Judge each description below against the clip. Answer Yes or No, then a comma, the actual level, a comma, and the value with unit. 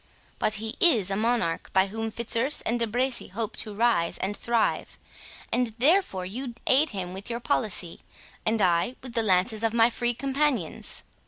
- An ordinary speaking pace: Yes, average, 175 wpm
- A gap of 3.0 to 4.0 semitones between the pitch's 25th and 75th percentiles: Yes, average, 3.4 semitones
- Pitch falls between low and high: No, high, 225 Hz